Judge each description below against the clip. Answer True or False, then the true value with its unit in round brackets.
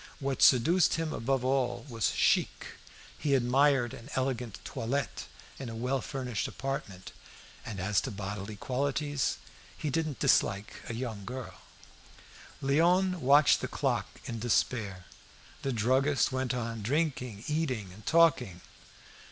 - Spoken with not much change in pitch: False (3.8 semitones)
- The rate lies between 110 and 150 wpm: True (140 wpm)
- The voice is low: True (130 Hz)